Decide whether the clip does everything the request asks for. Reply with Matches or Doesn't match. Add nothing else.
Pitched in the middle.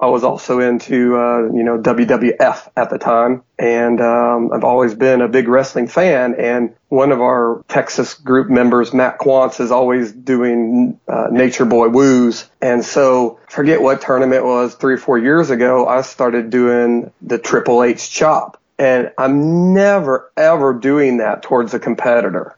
Doesn't match